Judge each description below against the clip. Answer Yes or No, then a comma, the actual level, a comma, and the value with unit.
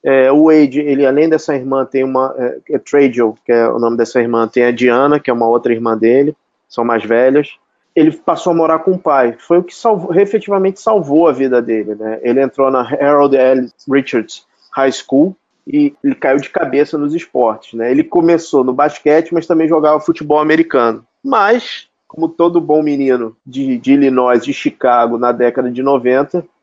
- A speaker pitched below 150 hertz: Yes, medium, 140 Hz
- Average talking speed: No, fast, 195 wpm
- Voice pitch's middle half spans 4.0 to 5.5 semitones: Yes, average, 4.6 semitones